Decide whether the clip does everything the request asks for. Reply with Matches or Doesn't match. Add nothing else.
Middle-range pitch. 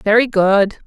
Doesn't match